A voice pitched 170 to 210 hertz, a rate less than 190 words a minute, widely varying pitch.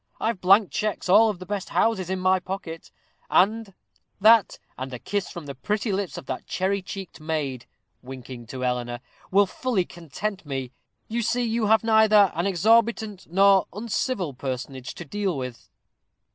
Yes: high, 190 Hz; average, 160 wpm; wide, 6.6 semitones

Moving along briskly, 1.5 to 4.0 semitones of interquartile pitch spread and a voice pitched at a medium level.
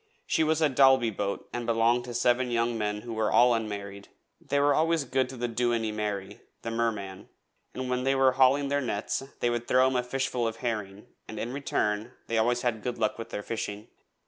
No: fast, 215 wpm; average, 2.8 semitones; low, 120 Hz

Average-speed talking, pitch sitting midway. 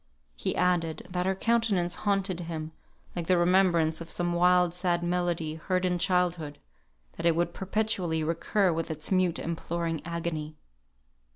Yes: average, 150 wpm; medium, 175 Hz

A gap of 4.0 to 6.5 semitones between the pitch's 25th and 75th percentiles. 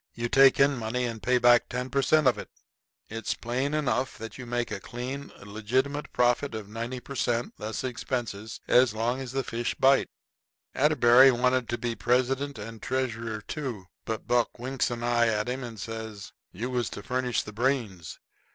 No: narrow, 2.4 semitones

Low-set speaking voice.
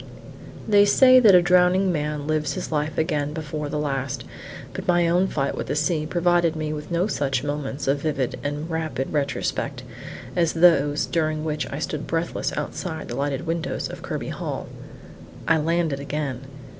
No: medium, 155 Hz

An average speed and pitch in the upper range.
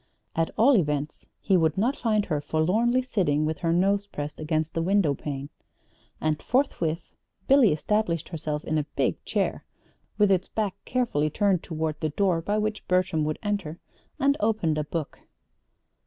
No: average, 165 wpm; medium, 170 Hz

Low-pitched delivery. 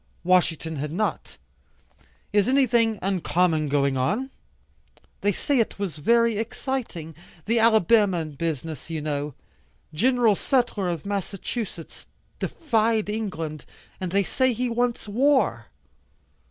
No: high, 200 Hz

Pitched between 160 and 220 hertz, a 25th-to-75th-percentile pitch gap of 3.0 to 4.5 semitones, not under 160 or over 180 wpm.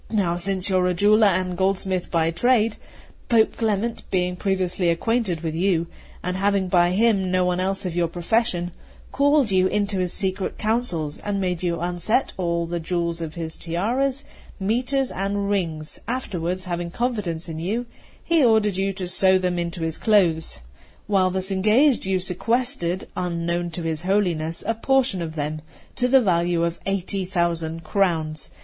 Yes: medium, 185 Hz; average, 3.4 semitones; average, 170 wpm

